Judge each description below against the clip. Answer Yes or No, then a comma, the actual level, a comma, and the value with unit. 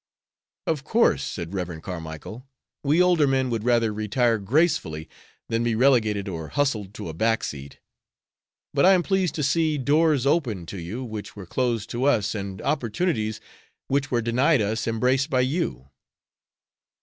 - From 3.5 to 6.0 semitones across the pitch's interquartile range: Yes, wide, 5.5 semitones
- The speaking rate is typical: Yes, average, 160 wpm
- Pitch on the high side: No, low, 120 Hz